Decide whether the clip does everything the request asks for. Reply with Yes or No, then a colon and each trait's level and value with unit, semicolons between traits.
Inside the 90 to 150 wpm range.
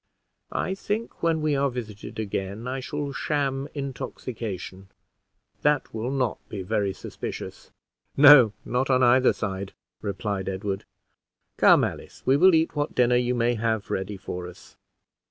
Yes: average, 145 wpm